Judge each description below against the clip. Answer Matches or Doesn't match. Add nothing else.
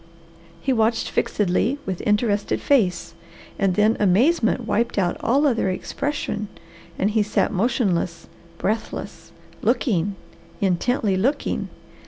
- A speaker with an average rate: Doesn't match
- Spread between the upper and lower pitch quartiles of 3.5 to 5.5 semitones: Matches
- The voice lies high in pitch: Matches